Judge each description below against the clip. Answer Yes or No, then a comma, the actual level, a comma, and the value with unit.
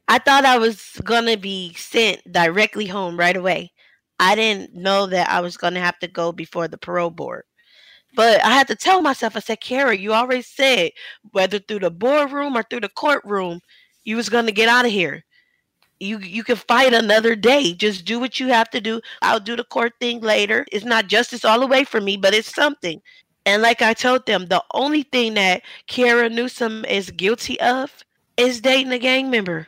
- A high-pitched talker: Yes, high, 225 Hz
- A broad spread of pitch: No, average, 4.2 semitones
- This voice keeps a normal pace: No, fast, 210 wpm